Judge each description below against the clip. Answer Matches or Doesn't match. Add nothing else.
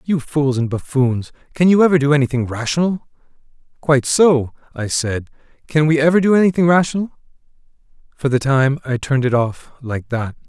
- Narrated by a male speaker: Matches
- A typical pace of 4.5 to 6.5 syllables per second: Matches